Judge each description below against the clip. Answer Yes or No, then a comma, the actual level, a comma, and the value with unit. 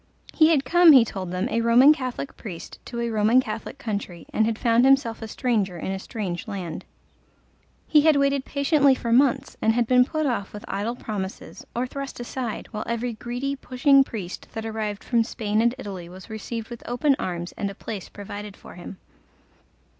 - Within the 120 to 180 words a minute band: No, average, 190 wpm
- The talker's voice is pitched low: No, high, 230 Hz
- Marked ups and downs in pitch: No, average, 4.1 semitones